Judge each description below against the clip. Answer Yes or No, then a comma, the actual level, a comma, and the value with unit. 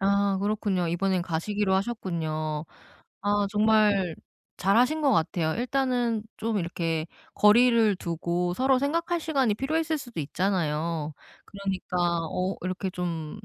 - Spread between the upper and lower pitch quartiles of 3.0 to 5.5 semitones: Yes, average, 5.1 semitones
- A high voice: Yes, high, 200 Hz